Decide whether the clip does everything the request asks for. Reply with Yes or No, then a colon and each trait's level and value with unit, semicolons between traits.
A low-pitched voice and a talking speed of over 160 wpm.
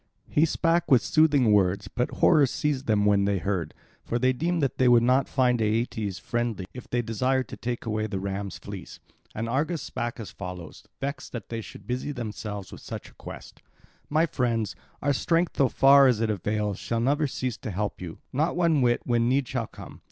Yes: low, 120 Hz; fast, 205 wpm